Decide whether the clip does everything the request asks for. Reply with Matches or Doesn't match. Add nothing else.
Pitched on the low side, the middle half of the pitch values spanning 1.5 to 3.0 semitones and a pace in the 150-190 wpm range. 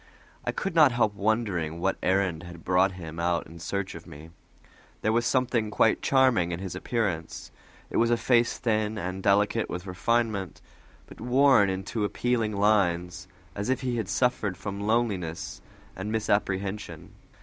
Doesn't match